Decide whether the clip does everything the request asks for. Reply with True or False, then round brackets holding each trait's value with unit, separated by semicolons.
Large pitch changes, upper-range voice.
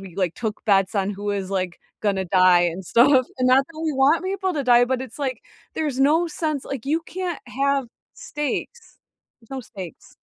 True (7.0 semitones; 255 Hz)